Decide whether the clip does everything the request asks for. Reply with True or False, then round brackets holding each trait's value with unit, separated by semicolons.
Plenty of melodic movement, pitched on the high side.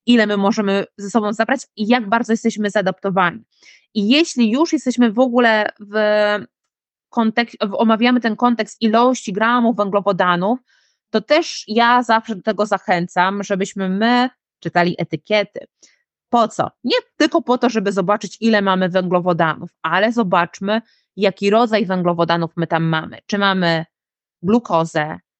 False (3.5 semitones; 215 Hz)